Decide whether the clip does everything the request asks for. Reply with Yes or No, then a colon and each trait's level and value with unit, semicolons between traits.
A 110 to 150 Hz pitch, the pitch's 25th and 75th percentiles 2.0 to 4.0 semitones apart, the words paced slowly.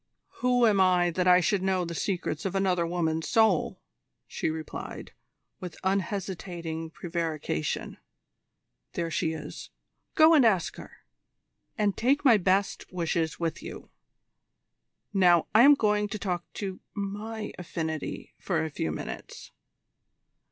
No: medium, 180 Hz; average, 3.6 semitones; slow, 130 wpm